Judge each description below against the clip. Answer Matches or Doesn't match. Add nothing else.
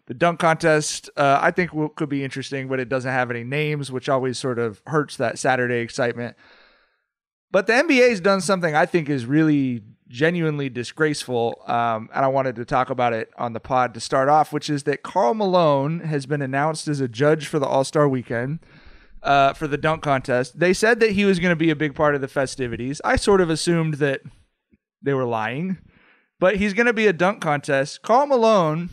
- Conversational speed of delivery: Doesn't match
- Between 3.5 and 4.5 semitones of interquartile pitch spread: Matches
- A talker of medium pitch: Matches